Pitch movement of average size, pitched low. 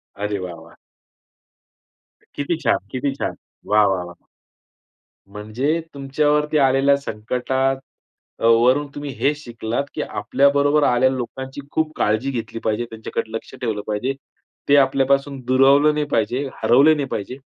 Yes: average, 3.9 semitones; low, 130 Hz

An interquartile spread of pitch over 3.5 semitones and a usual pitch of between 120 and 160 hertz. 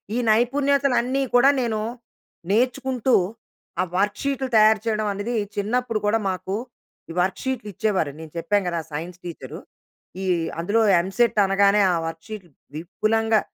No: average, 4.1 semitones; high, 215 Hz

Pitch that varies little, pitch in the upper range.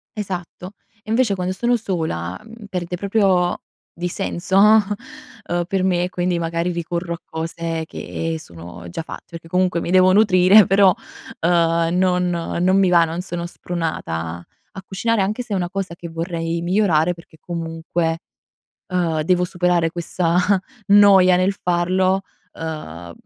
No: narrow, 2.3 semitones; medium, 180 Hz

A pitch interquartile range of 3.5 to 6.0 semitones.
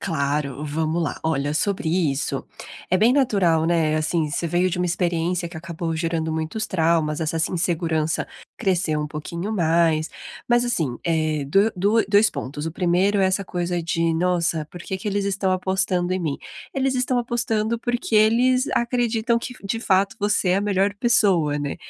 Yes: average, 4.2 semitones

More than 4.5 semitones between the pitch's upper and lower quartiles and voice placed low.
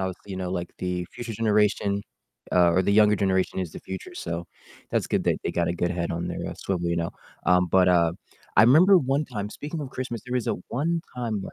Yes: average, 5.1 semitones; very low, 95 Hz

